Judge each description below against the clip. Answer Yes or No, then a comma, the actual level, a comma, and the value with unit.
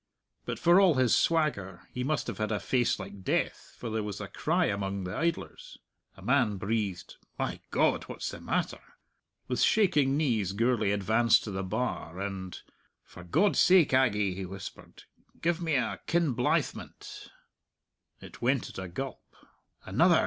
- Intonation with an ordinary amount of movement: No, wide, 6.2 semitones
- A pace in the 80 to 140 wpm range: No, average, 160 wpm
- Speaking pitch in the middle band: No, low, 110 Hz